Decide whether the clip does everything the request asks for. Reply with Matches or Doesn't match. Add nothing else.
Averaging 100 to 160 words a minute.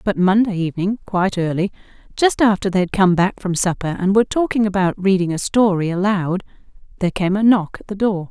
Doesn't match